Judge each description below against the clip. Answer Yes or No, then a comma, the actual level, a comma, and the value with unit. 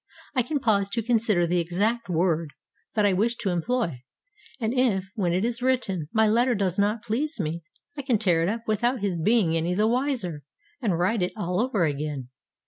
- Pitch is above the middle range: Yes, high, 205 Hz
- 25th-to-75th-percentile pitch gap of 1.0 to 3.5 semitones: No, average, 5.1 semitones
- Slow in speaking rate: No, average, 200 wpm